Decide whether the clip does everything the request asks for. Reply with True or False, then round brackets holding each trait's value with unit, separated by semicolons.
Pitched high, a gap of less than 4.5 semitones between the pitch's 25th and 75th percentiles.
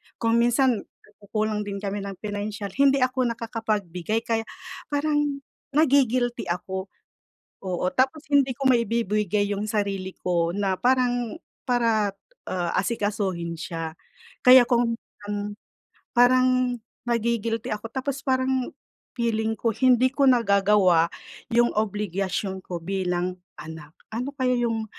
True (220 Hz; 3.8 semitones)